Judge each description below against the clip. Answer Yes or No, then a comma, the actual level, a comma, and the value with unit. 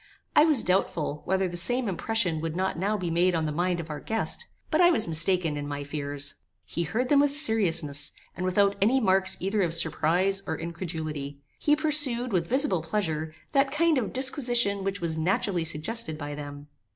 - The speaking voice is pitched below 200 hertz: Yes, medium, 185 Hz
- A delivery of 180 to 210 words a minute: Yes, average, 190 wpm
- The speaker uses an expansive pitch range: Yes, wide, 6.0 semitones